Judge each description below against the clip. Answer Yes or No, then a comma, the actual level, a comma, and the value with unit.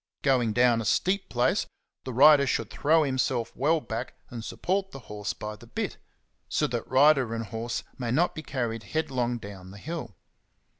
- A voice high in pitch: No, low, 125 Hz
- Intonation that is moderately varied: Yes, average, 4.4 semitones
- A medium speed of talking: Yes, average, 180 wpm